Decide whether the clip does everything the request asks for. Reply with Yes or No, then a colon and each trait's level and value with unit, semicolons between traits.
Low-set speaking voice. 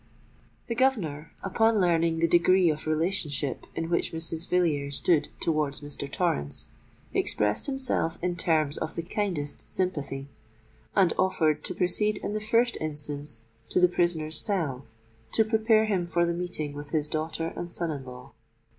No: medium, 165 Hz